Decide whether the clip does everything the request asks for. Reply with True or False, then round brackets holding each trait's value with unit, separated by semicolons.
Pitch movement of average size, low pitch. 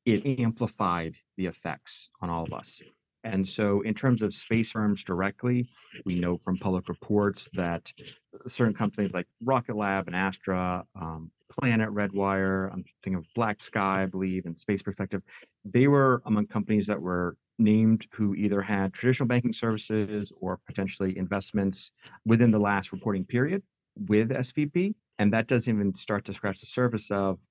True (3.1 semitones; 105 Hz)